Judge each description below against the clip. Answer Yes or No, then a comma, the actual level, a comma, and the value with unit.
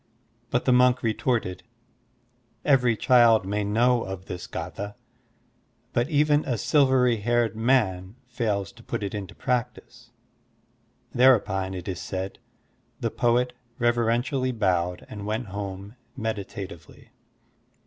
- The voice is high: No, low, 115 Hz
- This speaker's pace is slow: Yes, slow, 120 wpm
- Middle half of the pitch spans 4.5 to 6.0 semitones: No, average, 3.8 semitones